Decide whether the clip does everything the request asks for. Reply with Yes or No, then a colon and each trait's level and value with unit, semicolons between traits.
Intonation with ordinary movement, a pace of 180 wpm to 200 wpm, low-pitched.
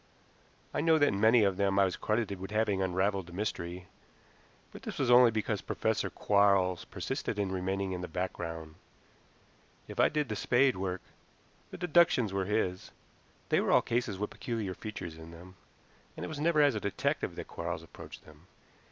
Yes: average, 3.4 semitones; average, 185 wpm; low, 100 Hz